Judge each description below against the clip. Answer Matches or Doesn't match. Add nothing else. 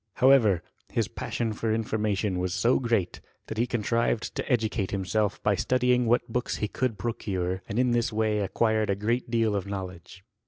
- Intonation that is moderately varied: Matches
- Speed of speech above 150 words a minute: Matches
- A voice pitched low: Matches